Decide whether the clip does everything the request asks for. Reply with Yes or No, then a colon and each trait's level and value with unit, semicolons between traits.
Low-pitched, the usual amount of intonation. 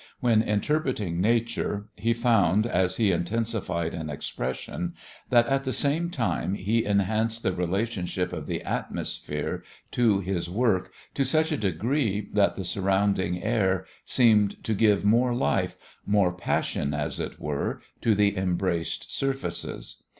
Yes: low, 105 Hz; average, 4.2 semitones